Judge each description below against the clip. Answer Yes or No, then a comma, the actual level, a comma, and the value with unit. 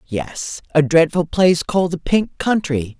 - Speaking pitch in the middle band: Yes, medium, 165 Hz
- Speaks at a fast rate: No, average, 160 wpm